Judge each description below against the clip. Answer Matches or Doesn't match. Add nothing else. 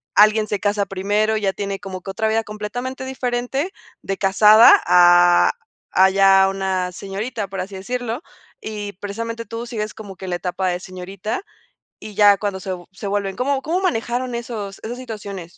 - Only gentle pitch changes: Doesn't match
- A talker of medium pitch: Doesn't match